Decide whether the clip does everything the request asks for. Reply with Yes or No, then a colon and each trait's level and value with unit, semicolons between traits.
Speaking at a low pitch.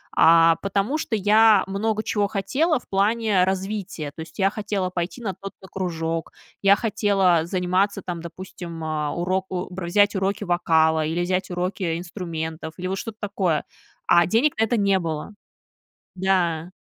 No: high, 190 Hz